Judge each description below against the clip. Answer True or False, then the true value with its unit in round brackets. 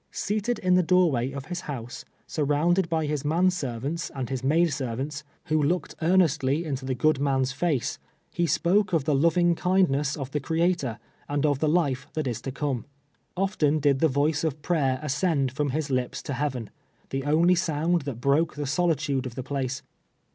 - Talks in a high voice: False (145 Hz)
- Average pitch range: True (3.8 semitones)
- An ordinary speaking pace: True (190 wpm)